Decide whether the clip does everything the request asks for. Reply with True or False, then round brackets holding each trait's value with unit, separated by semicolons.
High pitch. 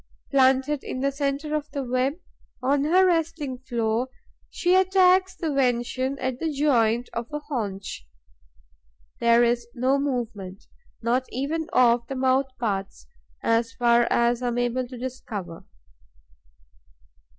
True (255 Hz)